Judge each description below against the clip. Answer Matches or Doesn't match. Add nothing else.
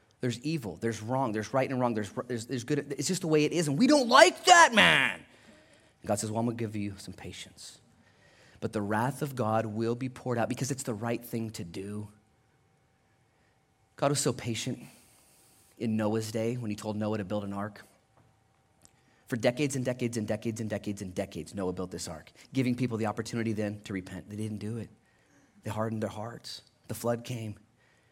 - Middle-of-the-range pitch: Doesn't match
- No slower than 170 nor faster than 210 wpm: Matches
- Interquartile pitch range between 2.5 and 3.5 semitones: Matches